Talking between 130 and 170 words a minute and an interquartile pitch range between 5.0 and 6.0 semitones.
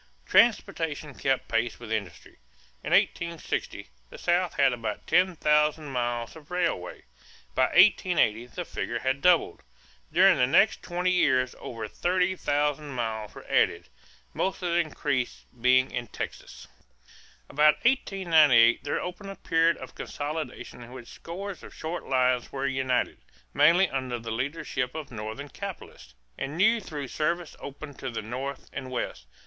Yes: average, 150 wpm; wide, 5.5 semitones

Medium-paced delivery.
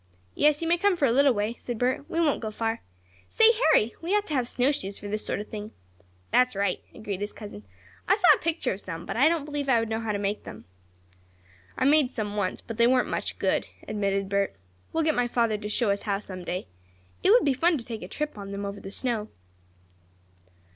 No: fast, 235 wpm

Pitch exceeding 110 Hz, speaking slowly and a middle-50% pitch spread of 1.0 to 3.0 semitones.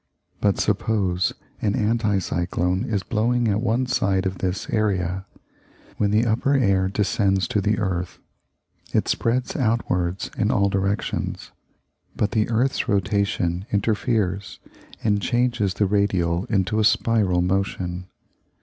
No: low, 100 Hz; slow, 130 wpm; average, 2.7 semitones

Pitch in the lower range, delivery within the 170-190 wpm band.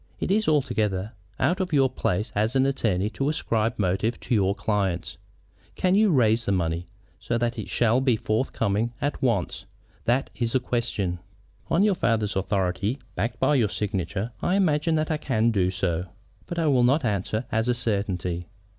Yes: low, 115 Hz; average, 180 wpm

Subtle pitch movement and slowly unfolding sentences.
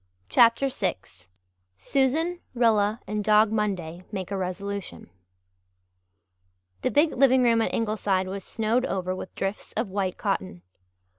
No: average, 3.7 semitones; slow, 130 wpm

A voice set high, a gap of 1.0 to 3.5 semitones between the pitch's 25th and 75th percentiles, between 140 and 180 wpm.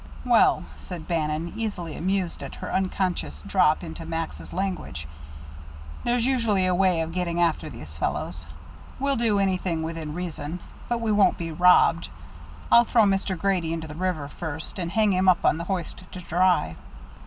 No: medium, 180 Hz; average, 3.2 semitones; average, 165 wpm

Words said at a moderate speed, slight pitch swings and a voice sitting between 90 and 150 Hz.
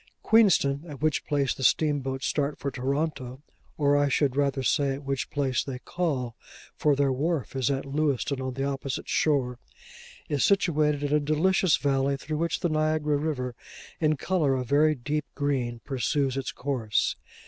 Yes: average, 170 wpm; narrow, 2.3 semitones; medium, 140 Hz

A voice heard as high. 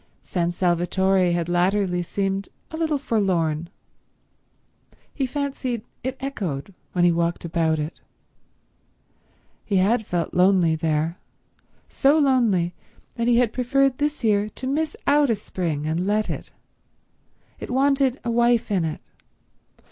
Yes: high, 200 Hz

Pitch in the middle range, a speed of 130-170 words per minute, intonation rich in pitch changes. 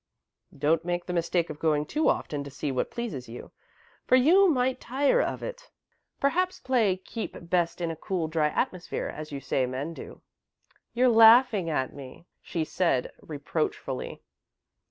Yes: medium, 170 Hz; average, 160 wpm; wide, 8.5 semitones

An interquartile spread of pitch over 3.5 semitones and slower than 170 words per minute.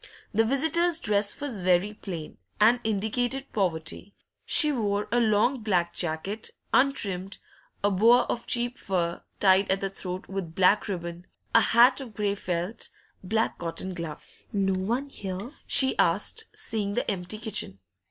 Yes: average, 4.2 semitones; average, 150 wpm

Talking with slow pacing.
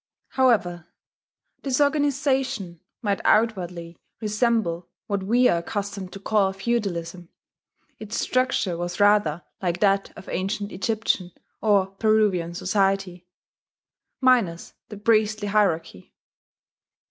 Yes: slow, 100 wpm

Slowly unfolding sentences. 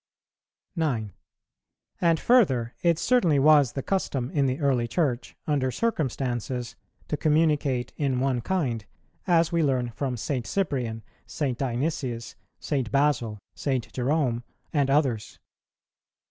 Yes: slow, 120 wpm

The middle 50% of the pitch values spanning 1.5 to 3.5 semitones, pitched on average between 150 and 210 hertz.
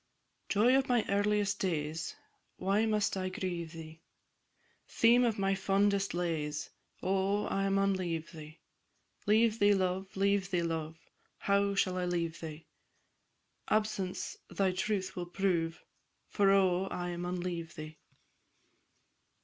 Yes: average, 2.8 semitones; high, 190 Hz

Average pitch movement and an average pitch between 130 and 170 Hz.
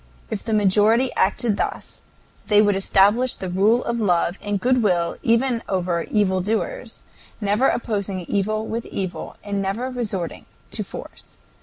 No: average, 3.2 semitones; high, 205 Hz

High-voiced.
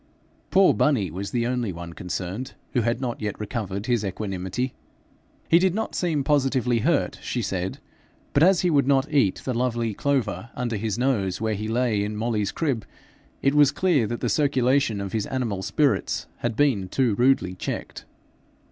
No: low, 120 Hz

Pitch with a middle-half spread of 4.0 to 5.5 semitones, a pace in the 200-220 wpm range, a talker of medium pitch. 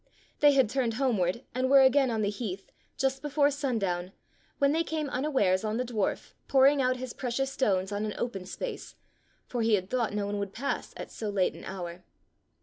No: average, 5.1 semitones; fast, 205 wpm; high, 240 Hz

